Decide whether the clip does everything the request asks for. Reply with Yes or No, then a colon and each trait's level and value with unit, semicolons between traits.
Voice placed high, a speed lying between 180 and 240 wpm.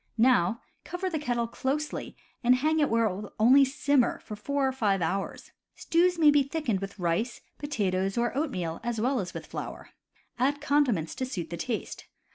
Yes: high, 245 Hz; average, 190 wpm